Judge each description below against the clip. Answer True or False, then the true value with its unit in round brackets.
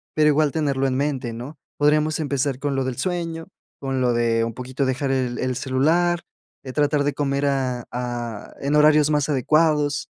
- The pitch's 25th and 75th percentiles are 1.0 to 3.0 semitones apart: True (2.7 semitones)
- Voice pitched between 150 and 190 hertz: False (140 Hz)